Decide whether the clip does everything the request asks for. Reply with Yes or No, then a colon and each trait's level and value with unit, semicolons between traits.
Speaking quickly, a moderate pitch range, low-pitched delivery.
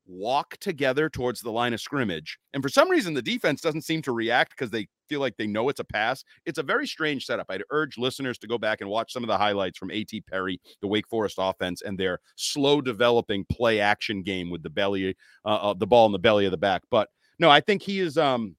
No: fast, 250 wpm; wide, 5.8 semitones; low, 115 Hz